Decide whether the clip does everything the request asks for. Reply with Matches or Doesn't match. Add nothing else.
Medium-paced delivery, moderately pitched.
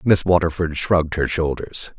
Doesn't match